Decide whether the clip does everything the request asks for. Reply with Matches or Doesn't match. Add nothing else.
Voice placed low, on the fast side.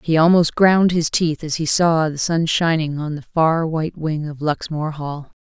Doesn't match